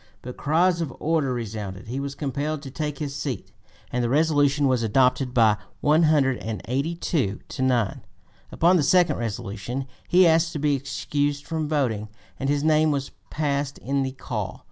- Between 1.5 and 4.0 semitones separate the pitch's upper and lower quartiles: Yes, average, 3.6 semitones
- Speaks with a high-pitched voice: No, medium, 140 Hz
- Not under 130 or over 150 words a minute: No, average, 165 wpm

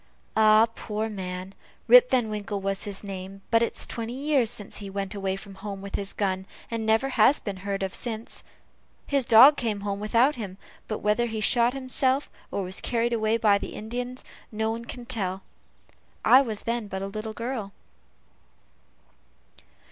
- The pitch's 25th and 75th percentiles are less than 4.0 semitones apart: Yes, average, 3.1 semitones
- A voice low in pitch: No, high, 215 Hz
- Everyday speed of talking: Yes, average, 170 wpm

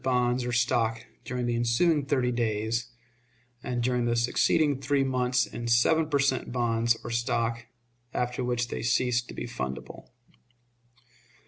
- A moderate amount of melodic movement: No, narrow, 1.4 semitones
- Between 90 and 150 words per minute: Yes, average, 145 wpm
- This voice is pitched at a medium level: No, low, 120 Hz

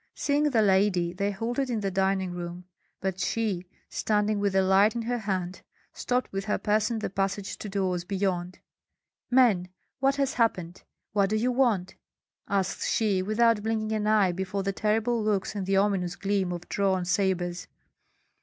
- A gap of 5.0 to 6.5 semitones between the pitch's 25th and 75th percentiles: No, narrow, 2.6 semitones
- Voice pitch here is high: Yes, high, 200 Hz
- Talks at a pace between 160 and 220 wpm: Yes, average, 170 wpm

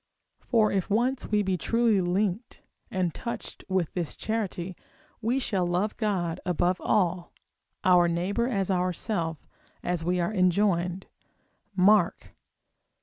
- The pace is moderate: No, slow, 130 wpm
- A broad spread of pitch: No, average, 3.2 semitones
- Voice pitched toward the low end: No, medium, 185 Hz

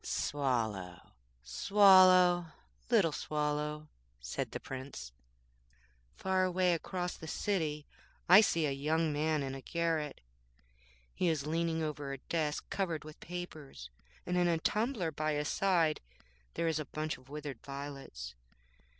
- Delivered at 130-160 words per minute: Yes, slow, 135 wpm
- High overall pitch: No, medium, 155 Hz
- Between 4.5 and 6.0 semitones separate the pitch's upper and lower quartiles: No, average, 4.0 semitones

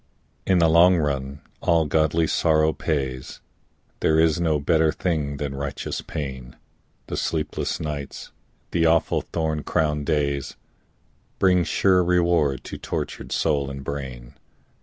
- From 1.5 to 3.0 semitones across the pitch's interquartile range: Yes, average, 2.7 semitones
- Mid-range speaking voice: No, very low, 75 Hz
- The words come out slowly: Yes, slow, 130 wpm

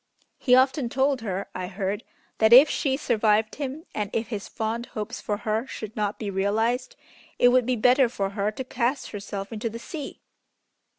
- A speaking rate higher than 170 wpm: Yes, average, 185 wpm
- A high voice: Yes, high, 225 Hz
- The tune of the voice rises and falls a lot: No, average, 3.5 semitones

